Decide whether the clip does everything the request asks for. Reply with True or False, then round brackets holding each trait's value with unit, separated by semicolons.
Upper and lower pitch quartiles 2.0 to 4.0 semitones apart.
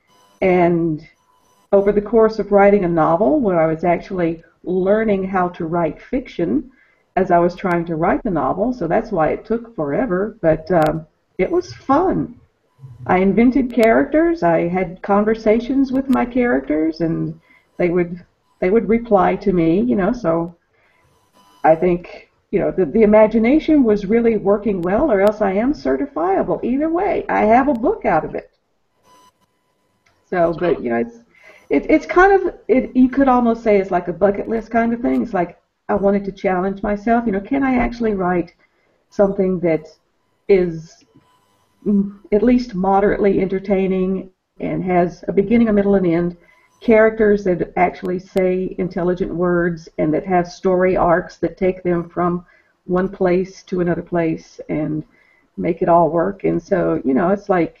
False (4.4 semitones)